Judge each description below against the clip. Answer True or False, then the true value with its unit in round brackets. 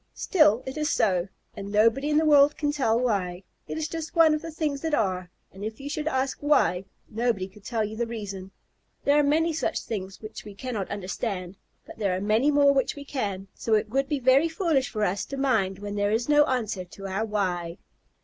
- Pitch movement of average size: False (6.4 semitones)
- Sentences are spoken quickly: True (225 wpm)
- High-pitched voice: True (230 Hz)